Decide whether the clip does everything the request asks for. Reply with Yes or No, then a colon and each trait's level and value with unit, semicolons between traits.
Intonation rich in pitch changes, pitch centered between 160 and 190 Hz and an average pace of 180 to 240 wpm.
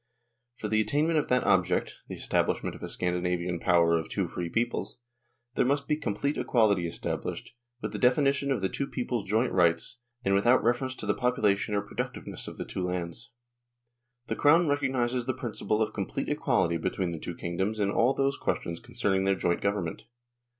No: wide, 5.8 semitones; low, 110 Hz; average, 190 wpm